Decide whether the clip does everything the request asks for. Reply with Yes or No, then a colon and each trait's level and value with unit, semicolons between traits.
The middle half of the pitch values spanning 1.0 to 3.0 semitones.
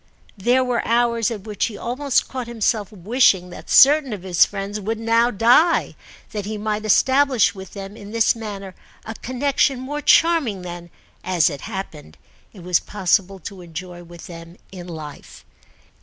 No: average, 4.7 semitones